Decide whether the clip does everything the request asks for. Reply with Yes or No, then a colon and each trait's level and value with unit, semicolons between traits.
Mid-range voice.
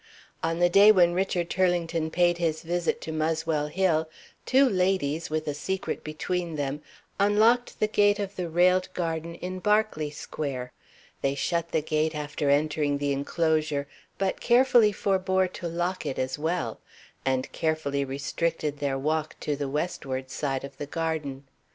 Yes: medium, 160 Hz